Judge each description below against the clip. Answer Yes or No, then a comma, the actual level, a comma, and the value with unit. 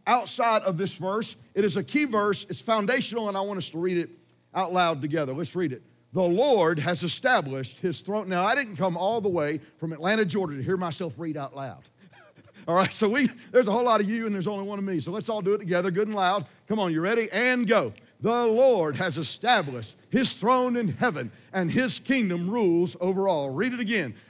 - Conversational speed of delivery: No, fast, 230 wpm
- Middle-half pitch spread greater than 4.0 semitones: Yes, average, 4.4 semitones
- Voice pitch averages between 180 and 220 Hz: Yes, high, 190 Hz